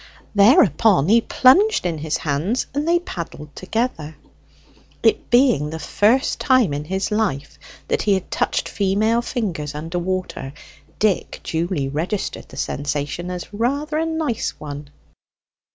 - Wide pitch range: Yes, wide, 7.5 semitones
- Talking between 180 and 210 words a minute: No, slow, 135 wpm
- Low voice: No, high, 190 Hz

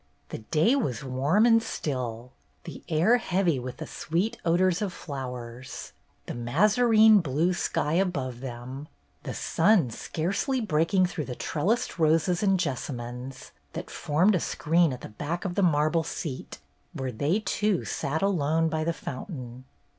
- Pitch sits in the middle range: Yes, medium, 160 Hz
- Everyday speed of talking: Yes, average, 150 wpm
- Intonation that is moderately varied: No, wide, 6.2 semitones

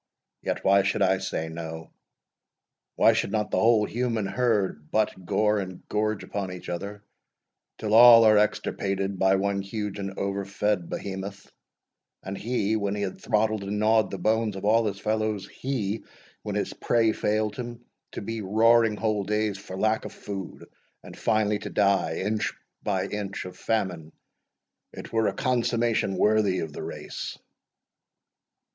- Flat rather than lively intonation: Yes, narrow, 2.1 semitones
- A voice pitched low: Yes, low, 105 Hz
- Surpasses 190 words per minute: No, average, 160 wpm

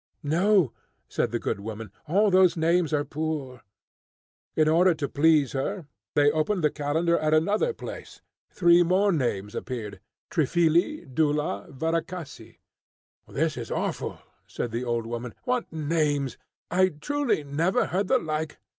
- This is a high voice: No, medium, 155 Hz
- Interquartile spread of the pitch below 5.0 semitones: Yes, average, 4.2 semitones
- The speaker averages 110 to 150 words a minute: Yes, average, 145 wpm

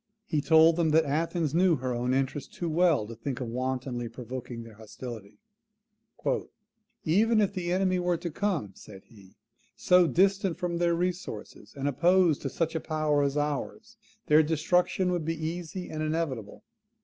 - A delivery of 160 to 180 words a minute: Yes, average, 165 wpm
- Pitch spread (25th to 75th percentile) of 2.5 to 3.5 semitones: No, average, 5.3 semitones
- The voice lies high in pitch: No, medium, 155 Hz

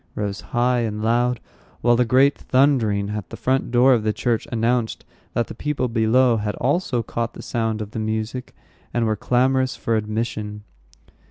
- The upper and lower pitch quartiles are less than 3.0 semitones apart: Yes, narrow, 2.5 semitones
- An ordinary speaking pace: Yes, average, 175 wpm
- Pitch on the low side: Yes, low, 115 Hz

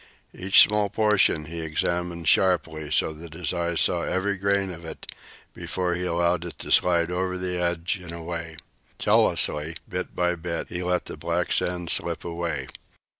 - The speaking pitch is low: Yes, very low, 85 Hz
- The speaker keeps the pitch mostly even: Yes, narrow, 1.4 semitones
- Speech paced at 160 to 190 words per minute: Yes, average, 170 wpm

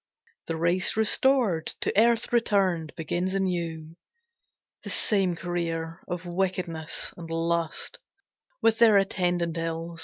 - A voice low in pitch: No, medium, 175 Hz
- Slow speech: Yes, slow, 115 wpm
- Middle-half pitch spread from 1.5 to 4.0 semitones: Yes, average, 2.9 semitones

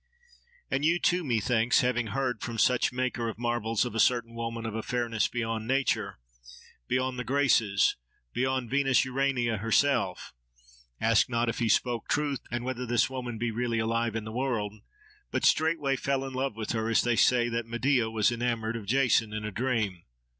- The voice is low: Yes, low, 120 Hz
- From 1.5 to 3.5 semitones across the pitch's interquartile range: Yes, narrow, 2.5 semitones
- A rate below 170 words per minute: No, average, 180 wpm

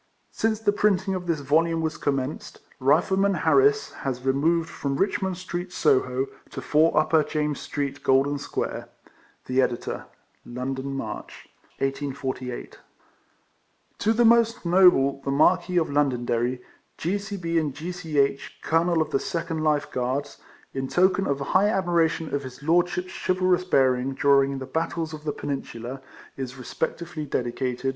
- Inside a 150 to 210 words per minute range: No, average, 140 wpm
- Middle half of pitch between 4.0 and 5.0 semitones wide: Yes, average, 4.6 semitones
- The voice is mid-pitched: Yes, medium, 150 Hz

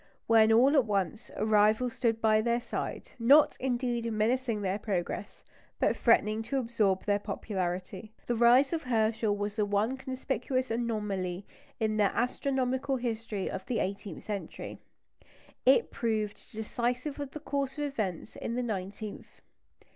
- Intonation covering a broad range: No, average, 3.2 semitones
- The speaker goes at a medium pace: Yes, average, 145 wpm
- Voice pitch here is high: Yes, high, 225 Hz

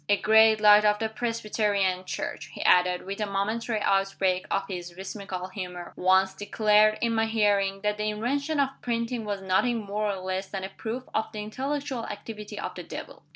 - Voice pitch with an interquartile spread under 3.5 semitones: Yes, narrow, 2.5 semitones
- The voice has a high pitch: Yes, high, 210 Hz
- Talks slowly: No, average, 190 wpm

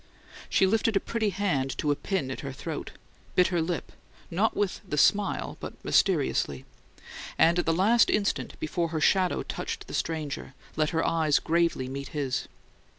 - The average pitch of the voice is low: No, medium, 165 Hz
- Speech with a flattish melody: No, average, 4.7 semitones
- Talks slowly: No, average, 170 wpm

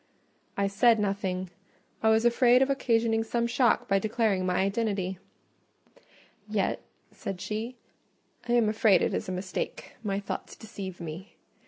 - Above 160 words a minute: No, average, 145 wpm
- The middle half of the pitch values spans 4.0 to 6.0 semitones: No, average, 3.2 semitones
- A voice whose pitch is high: Yes, high, 210 Hz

